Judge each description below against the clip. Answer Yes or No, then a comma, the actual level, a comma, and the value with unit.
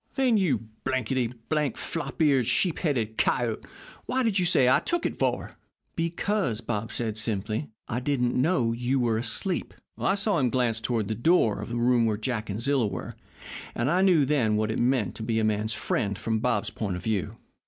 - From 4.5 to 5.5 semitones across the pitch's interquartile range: Yes, average, 5.2 semitones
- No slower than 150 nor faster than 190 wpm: No, average, 200 wpm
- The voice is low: Yes, low, 120 Hz